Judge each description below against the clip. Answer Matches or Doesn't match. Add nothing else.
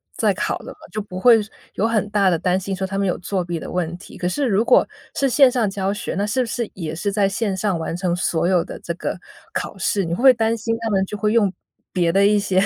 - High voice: Matches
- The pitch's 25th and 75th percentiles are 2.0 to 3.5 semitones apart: Matches